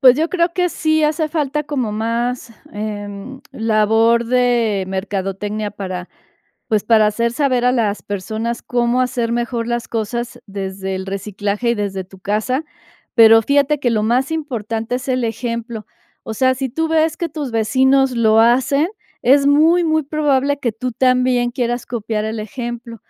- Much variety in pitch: No, average, 3.6 semitones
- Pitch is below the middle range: No, high, 235 Hz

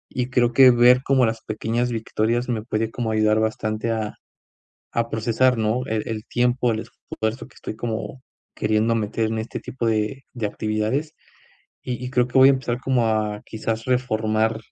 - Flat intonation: Yes, narrow, 2.2 semitones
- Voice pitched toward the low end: Yes, low, 115 Hz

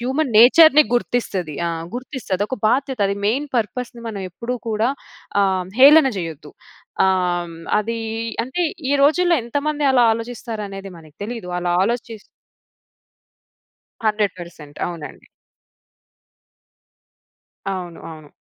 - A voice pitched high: Yes, high, 225 Hz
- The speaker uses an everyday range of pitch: No, wide, 6.1 semitones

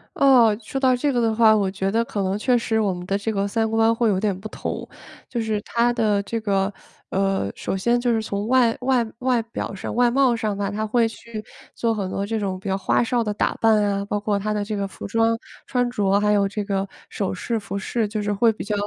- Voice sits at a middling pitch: No, high, 215 Hz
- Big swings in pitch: No, narrow, 2.5 semitones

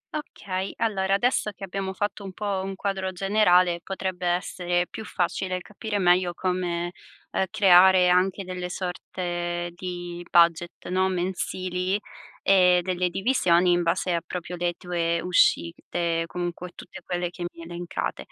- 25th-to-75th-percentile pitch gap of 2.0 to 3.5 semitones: No, narrow, 1.5 semitones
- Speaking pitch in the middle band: Yes, medium, 180 Hz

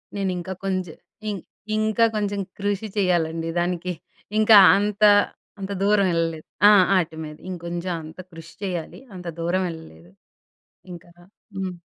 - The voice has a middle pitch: Yes, medium, 180 Hz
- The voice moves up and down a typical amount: Yes, average, 3.1 semitones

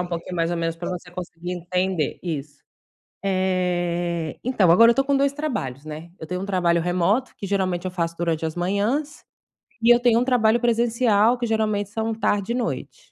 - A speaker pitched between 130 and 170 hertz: No, medium, 185 Hz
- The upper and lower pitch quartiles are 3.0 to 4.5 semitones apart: No, average, 4.9 semitones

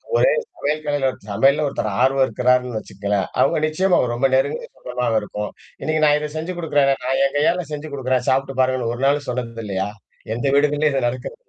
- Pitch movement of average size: Yes, average, 3.4 semitones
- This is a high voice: No, low, 135 Hz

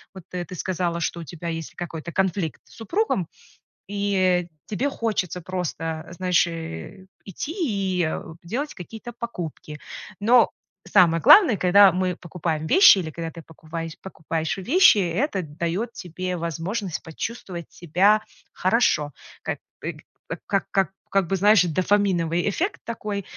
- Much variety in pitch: No, average, 3.4 semitones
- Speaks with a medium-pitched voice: Yes, medium, 180 Hz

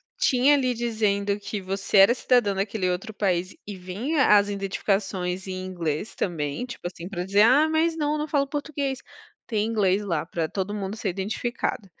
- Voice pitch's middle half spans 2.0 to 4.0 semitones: No, average, 4.9 semitones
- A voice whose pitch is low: No, high, 205 Hz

